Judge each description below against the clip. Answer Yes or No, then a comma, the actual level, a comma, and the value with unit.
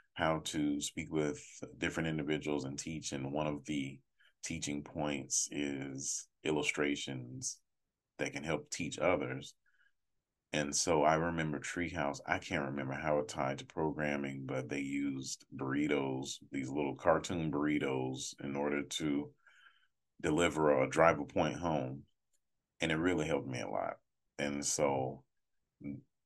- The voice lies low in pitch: Yes, very low, 75 Hz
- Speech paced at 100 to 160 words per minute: Yes, slow, 135 wpm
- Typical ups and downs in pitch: No, narrow, 1.8 semitones